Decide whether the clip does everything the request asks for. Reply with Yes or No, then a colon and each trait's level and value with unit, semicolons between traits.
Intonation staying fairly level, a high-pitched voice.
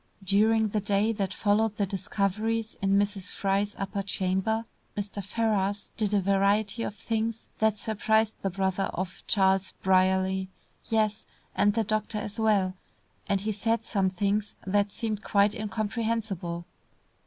Yes: narrow, 2.0 semitones; high, 205 Hz